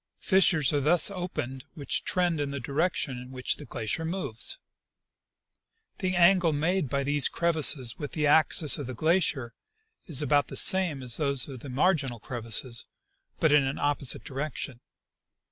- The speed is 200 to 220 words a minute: No, average, 160 wpm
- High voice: No, medium, 145 Hz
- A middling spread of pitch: Yes, average, 4.0 semitones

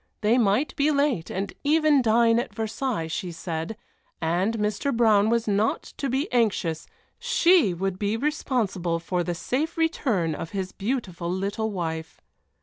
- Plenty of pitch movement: Yes, wide, 6.0 semitones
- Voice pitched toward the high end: Yes, high, 215 Hz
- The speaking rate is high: No, average, 150 wpm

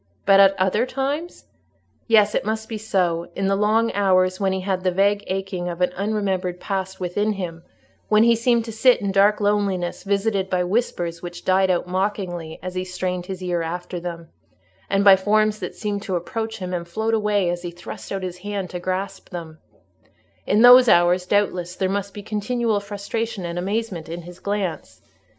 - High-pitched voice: Yes, high, 195 Hz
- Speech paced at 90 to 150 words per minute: No, average, 185 wpm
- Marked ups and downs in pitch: No, narrow, 2.6 semitones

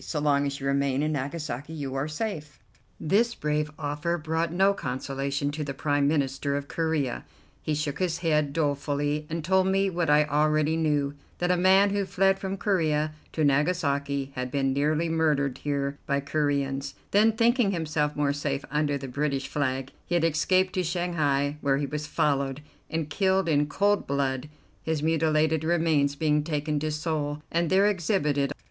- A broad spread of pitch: No, average, 2.8 semitones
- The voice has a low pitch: No, medium, 150 Hz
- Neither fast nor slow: Yes, average, 175 wpm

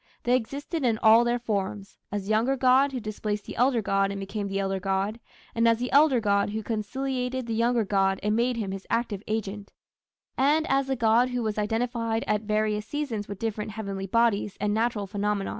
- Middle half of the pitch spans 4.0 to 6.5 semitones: No, average, 3.0 semitones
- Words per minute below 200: No, fast, 205 wpm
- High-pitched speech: Yes, high, 220 Hz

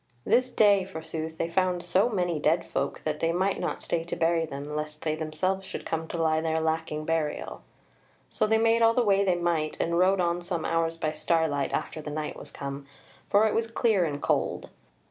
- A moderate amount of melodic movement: Yes, average, 3.4 semitones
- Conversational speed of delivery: No, fast, 210 wpm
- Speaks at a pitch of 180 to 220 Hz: No, medium, 165 Hz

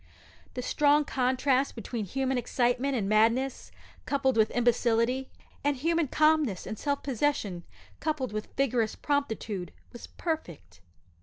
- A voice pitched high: Yes, very high, 255 Hz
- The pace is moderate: No, slow, 125 wpm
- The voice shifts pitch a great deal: No, average, 4.0 semitones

